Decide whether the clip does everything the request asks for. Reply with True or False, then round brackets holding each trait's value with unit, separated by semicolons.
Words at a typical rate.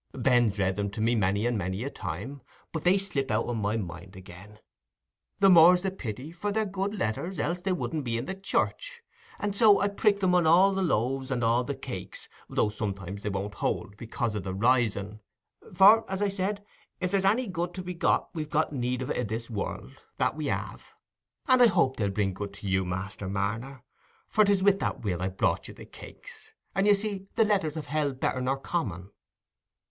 False (210 wpm)